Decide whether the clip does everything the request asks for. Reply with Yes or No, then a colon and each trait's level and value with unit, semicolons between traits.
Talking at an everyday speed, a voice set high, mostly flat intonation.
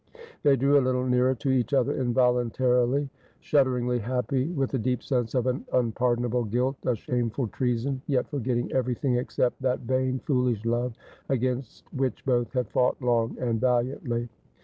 No: average, 160 wpm; low, 125 Hz; narrow, 1.4 semitones